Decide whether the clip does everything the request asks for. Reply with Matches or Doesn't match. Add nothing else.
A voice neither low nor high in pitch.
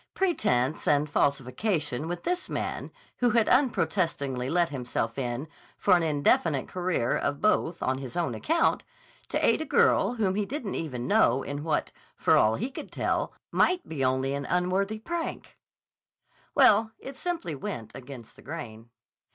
Matches